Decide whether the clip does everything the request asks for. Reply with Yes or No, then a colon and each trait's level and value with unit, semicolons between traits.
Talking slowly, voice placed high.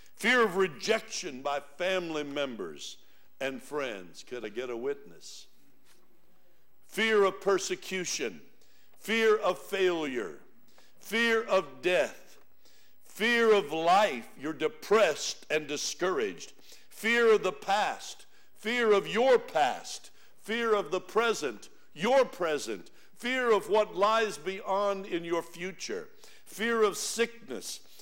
Yes: slow, 115 wpm; high, 205 Hz